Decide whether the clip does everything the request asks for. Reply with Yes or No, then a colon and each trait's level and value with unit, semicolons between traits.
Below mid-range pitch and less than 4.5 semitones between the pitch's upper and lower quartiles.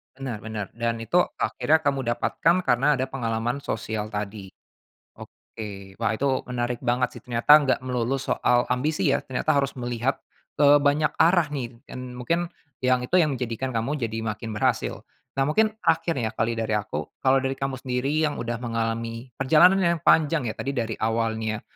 Yes: low, 125 Hz; average, 3.8 semitones